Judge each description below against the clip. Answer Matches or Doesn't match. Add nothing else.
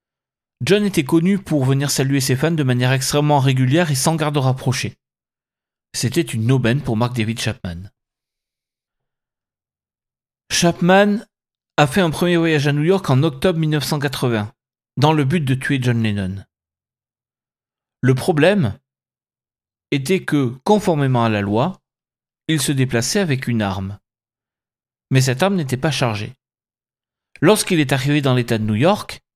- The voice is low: Matches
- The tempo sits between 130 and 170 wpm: Matches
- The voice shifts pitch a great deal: Doesn't match